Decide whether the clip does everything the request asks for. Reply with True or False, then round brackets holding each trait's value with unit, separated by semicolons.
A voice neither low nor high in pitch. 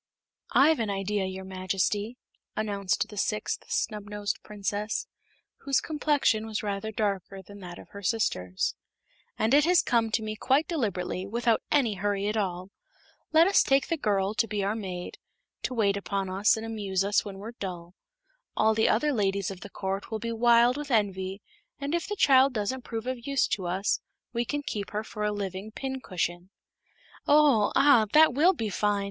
False (210 Hz)